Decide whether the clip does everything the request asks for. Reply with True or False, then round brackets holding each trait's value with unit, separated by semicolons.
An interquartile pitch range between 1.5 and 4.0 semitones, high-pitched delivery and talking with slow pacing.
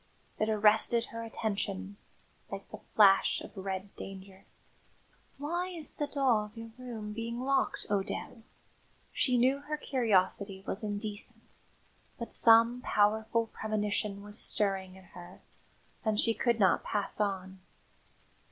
True (2.9 semitones; 215 Hz; 130 wpm)